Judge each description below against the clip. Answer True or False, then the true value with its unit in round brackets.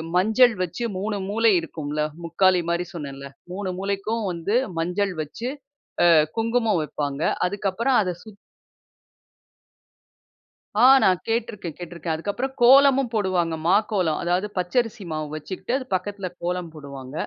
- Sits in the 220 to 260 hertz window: False (185 Hz)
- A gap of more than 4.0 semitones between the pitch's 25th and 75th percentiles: True (4.6 semitones)